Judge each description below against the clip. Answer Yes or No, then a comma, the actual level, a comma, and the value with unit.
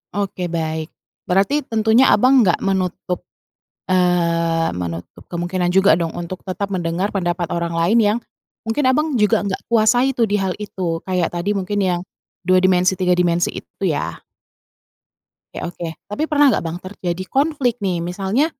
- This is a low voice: No, medium, 185 Hz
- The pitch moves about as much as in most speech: Yes, average, 3.4 semitones